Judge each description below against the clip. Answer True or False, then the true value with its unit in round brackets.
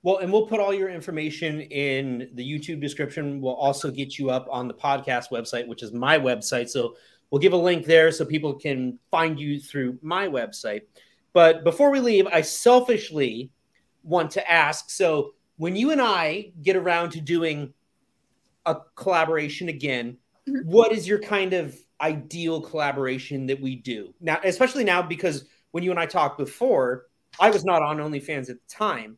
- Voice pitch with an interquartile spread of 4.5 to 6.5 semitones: True (5.1 semitones)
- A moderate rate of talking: True (180 wpm)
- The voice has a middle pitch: True (160 Hz)